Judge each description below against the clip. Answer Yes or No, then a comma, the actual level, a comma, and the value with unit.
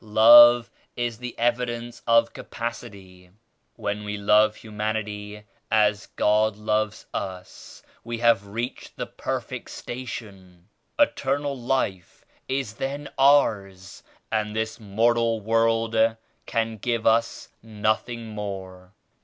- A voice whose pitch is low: Yes, low, 110 Hz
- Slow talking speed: Yes, slow, 110 wpm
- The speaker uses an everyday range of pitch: No, narrow, 2.2 semitones